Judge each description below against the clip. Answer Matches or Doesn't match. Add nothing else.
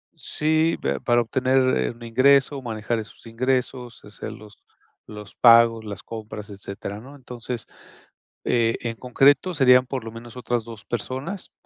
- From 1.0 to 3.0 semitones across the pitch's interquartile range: Matches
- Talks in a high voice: Doesn't match